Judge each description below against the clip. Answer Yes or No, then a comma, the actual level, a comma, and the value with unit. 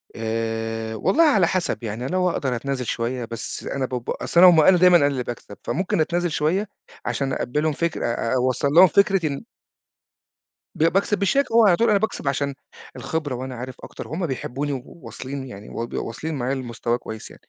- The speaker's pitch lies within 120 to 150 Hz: Yes, medium, 140 Hz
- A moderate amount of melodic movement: No, wide, 6.2 semitones